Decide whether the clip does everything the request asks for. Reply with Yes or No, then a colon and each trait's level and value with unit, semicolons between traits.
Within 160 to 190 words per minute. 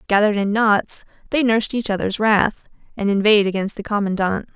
Yes: average, 170 wpm